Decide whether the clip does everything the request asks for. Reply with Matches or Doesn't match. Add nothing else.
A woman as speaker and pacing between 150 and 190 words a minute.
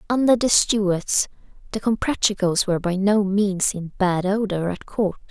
Matches